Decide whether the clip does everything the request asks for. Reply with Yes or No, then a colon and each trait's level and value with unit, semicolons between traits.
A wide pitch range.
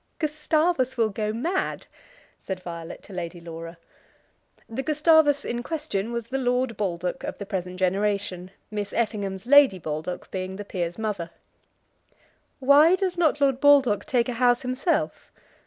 Yes: wide, 7.0 semitones